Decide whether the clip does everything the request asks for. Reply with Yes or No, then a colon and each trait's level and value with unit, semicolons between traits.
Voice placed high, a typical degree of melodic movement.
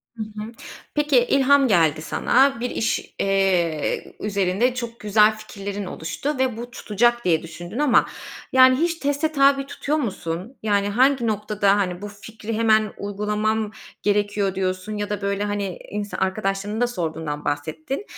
Yes: high, 210 Hz; average, 3.8 semitones